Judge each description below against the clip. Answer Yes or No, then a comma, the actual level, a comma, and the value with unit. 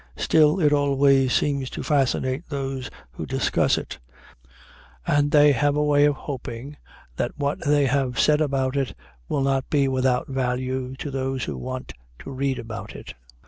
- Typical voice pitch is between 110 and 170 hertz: Yes, low, 135 Hz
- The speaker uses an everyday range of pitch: No, narrow, 1.9 semitones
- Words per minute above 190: No, average, 165 wpm